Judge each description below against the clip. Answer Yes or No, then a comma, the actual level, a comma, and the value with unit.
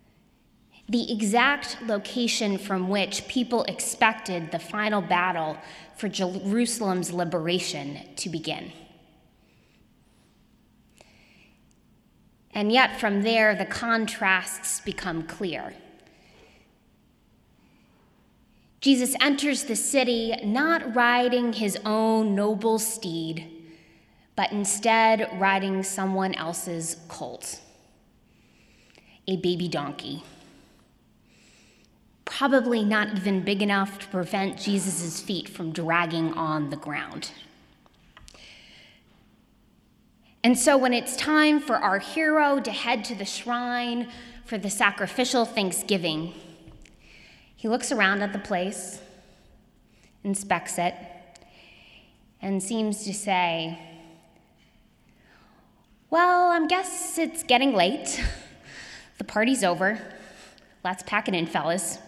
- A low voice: No, high, 200 Hz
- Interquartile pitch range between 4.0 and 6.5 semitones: Yes, average, 4.8 semitones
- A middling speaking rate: No, slow, 95 wpm